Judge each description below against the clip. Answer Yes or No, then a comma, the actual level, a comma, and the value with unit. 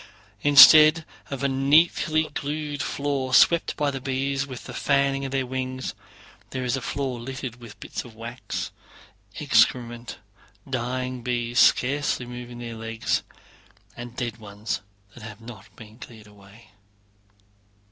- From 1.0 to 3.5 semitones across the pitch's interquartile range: Yes, average, 2.8 semitones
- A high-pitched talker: No, low, 130 Hz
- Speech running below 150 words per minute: Yes, slow, 135 wpm